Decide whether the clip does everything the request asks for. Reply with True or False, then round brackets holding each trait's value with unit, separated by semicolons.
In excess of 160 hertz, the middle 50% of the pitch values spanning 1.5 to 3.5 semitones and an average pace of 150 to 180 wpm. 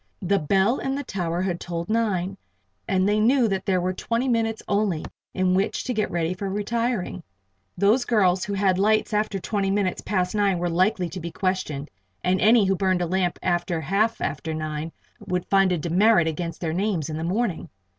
False (190 Hz; 3.2 semitones; 195 wpm)